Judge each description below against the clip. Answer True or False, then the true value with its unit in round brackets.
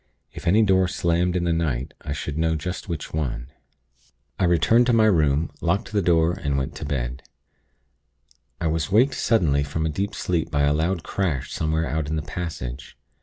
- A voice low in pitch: True (80 Hz)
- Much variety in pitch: False (3.6 semitones)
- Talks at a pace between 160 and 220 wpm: True (190 wpm)